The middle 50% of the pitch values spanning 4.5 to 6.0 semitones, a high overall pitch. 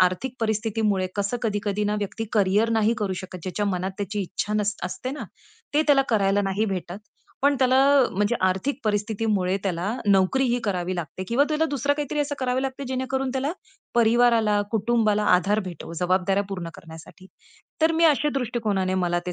Yes: average, 4.8 semitones; high, 210 Hz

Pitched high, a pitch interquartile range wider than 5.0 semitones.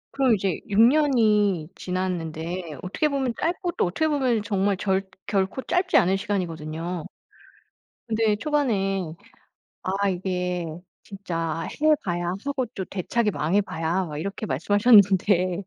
No: high, 195 Hz; average, 4.0 semitones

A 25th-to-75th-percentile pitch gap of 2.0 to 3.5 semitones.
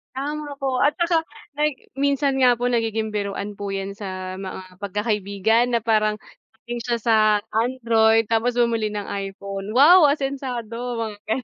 No: average, 4.2 semitones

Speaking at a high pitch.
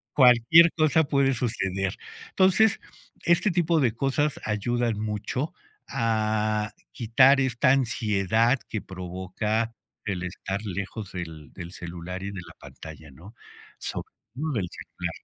No: low, 110 Hz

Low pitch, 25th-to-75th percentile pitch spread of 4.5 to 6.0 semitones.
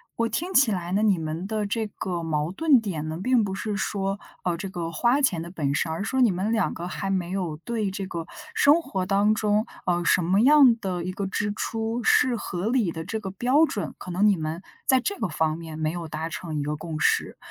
No: high, 195 Hz; average, 4.8 semitones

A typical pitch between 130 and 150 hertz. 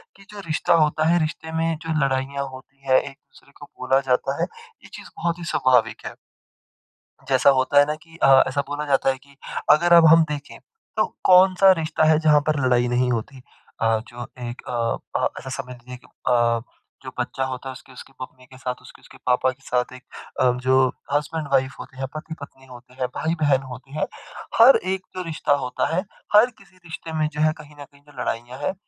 Yes: medium, 140 Hz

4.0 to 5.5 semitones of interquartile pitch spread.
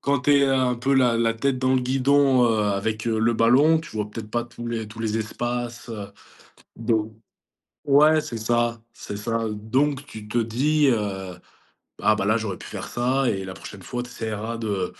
No: average, 3.0 semitones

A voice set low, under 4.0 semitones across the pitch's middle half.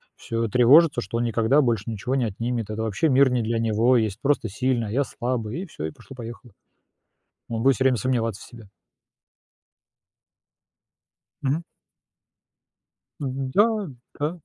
Yes: low, 120 Hz; average, 2.9 semitones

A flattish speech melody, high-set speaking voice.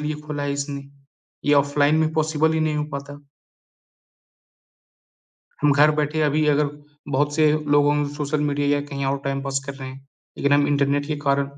No: narrow, 1.2 semitones; medium, 145 Hz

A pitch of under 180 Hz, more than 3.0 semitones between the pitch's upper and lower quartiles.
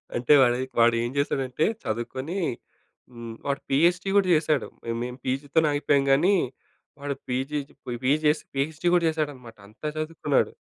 Yes: medium, 140 Hz; average, 3.7 semitones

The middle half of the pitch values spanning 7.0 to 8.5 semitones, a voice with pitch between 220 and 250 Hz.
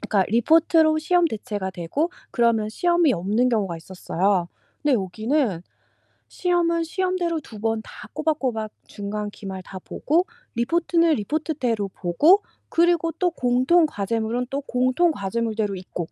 Yes: wide, 7.9 semitones; high, 245 Hz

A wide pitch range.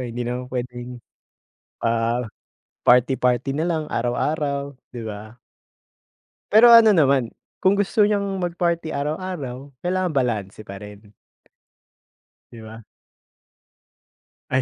Yes: wide, 6.3 semitones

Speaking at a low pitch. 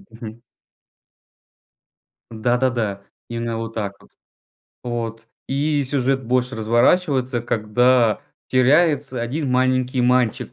Yes: low, 125 Hz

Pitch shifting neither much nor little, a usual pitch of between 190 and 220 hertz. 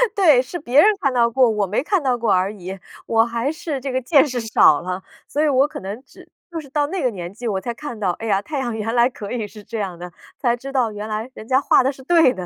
No: average, 4.7 semitones; high, 240 Hz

